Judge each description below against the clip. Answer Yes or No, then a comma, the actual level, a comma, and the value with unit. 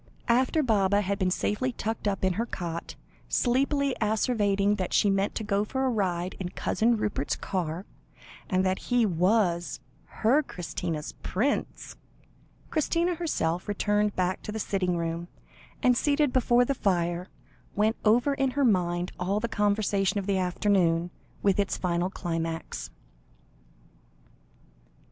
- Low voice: No, high, 200 Hz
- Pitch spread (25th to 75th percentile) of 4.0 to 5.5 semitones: Yes, average, 4.6 semitones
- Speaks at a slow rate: No, average, 145 wpm